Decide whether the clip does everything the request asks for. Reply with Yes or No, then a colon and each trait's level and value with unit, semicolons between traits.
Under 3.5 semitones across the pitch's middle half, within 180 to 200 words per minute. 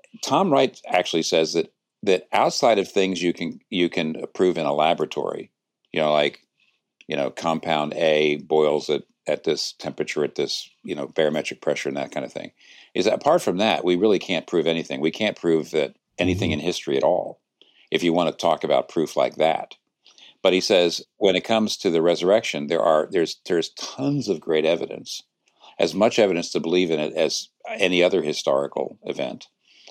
Yes: average, 2.8 semitones; average, 195 wpm